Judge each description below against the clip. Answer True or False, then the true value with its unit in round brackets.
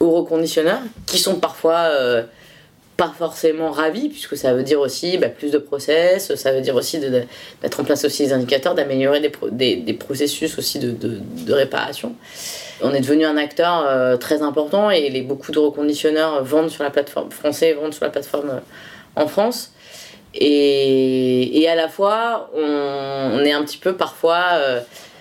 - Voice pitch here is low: False (150 Hz)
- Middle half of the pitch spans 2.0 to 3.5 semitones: True (2.9 semitones)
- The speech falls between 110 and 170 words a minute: False (195 wpm)